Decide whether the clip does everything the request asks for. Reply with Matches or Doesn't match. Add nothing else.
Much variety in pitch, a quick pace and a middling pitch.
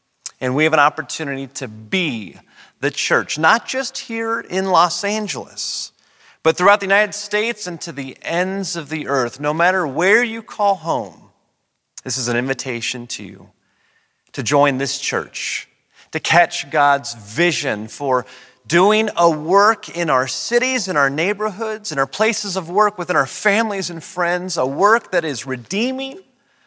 Doesn't match